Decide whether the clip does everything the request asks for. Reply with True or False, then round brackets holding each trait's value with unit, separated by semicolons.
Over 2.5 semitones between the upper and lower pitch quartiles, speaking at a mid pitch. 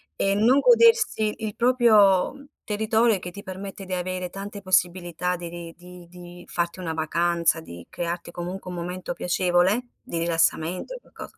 True (2.9 semitones; 180 Hz)